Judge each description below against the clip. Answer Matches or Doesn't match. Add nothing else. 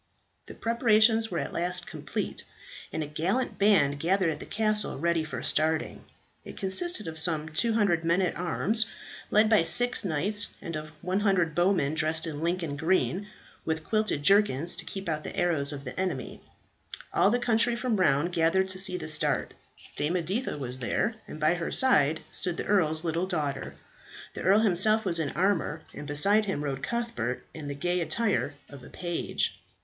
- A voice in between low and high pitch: Matches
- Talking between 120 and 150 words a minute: Doesn't match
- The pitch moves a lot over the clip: Doesn't match